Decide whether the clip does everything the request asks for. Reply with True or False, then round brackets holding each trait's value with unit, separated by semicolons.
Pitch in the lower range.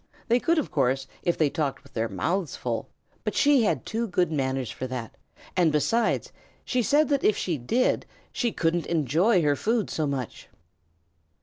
False (165 Hz)